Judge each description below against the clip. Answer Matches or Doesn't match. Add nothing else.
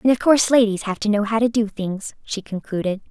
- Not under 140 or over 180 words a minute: Doesn't match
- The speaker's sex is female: Matches